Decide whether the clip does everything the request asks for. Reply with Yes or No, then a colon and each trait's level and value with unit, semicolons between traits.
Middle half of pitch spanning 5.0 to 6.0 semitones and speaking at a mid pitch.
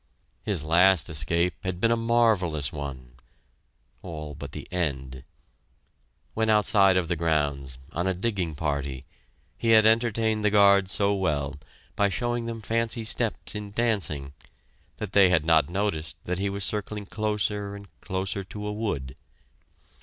No: wide, 5.5 semitones; very low, 95 Hz